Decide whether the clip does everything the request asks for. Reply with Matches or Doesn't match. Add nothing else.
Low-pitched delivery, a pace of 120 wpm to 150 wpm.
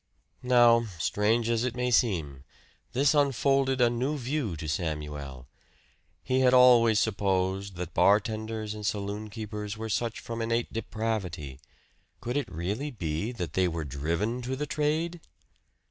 Matches